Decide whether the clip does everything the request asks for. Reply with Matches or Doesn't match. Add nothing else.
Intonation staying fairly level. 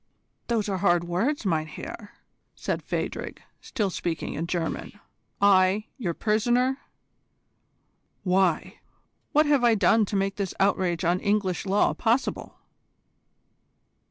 Doesn't match